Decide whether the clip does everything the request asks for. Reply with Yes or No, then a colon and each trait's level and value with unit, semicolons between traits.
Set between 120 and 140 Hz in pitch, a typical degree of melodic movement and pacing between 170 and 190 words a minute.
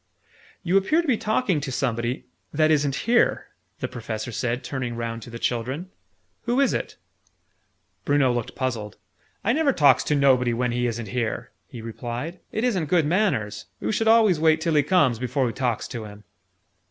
No: low, 135 Hz; wide, 7.0 semitones; average, 180 wpm